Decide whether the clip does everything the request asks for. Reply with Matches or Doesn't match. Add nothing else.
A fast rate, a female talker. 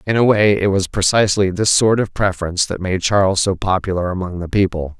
Doesn't match